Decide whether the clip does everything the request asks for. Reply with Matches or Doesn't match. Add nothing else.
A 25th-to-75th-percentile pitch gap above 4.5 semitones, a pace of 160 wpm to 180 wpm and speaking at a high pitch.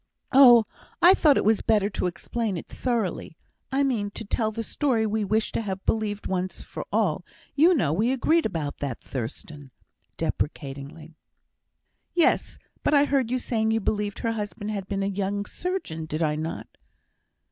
Matches